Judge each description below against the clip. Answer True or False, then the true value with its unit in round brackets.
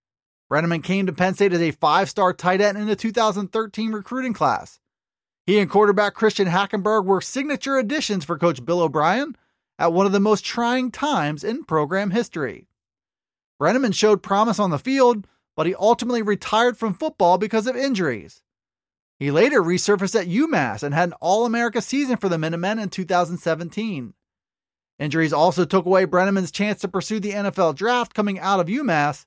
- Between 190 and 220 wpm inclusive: False (170 wpm)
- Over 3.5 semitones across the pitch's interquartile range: True (4.1 semitones)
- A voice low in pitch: False (200 Hz)